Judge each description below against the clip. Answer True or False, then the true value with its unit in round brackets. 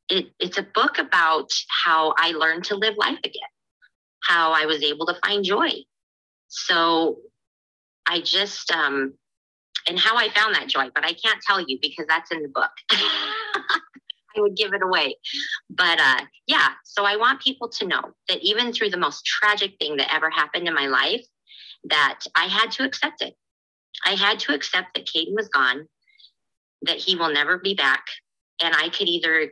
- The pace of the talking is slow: False (185 wpm)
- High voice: True (205 Hz)